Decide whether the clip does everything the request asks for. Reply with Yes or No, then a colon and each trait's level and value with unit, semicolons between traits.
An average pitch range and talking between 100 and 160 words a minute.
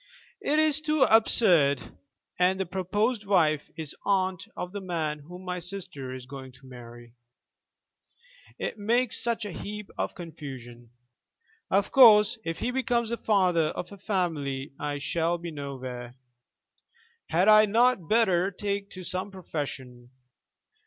No: wide, 6.4 semitones; average, 140 wpm